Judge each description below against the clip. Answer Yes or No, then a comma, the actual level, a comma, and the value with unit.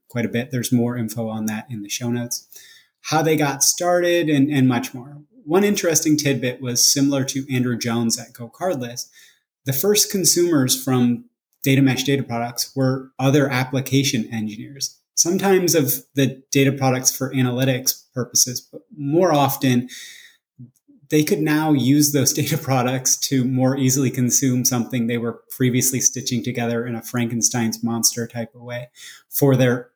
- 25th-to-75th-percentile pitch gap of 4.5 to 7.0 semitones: No, average, 2.7 semitones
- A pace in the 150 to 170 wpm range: Yes, average, 160 wpm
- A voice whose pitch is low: Yes, low, 130 Hz